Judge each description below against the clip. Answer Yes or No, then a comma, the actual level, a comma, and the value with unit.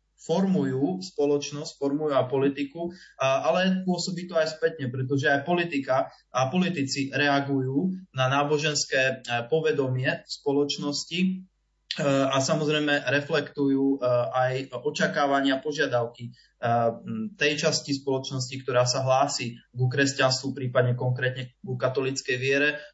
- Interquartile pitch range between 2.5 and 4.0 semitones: Yes, average, 2.8 semitones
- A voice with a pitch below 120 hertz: No, medium, 140 Hz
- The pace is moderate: No, slow, 105 wpm